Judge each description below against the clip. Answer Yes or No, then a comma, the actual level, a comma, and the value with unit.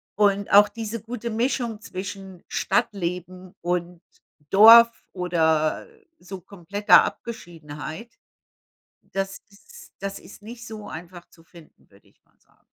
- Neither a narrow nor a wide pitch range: Yes, average, 3.8 semitones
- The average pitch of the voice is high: Yes, high, 195 Hz